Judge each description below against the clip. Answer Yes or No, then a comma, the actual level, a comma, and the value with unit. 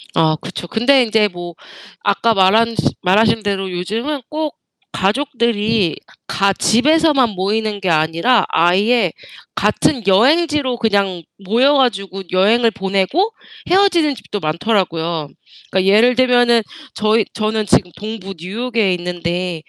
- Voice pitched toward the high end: Yes, high, 215 Hz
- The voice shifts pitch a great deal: No, average, 4.5 semitones